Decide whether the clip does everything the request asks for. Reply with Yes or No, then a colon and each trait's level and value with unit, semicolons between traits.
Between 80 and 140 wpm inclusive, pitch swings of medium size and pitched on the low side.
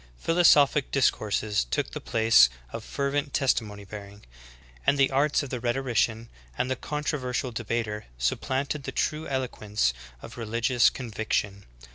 Yes: slow, 135 wpm; average, 4.3 semitones; low, 120 Hz